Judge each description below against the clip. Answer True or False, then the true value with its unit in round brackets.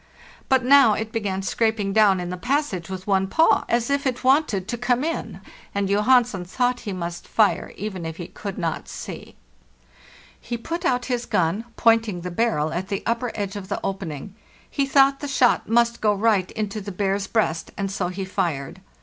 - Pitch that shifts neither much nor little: True (4.4 semitones)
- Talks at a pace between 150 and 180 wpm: False (190 wpm)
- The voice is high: True (210 Hz)